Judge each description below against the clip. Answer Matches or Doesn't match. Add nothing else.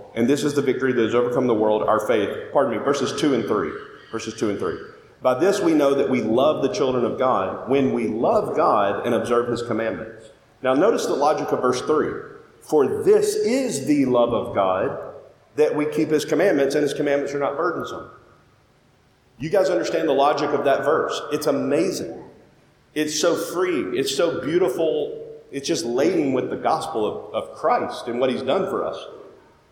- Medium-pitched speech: Matches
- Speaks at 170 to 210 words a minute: Matches